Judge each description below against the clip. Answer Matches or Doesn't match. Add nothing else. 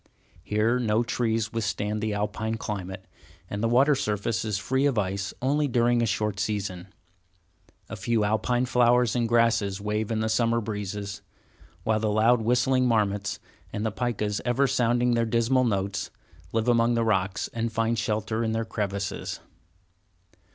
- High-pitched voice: Doesn't match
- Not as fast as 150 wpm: Doesn't match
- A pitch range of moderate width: Doesn't match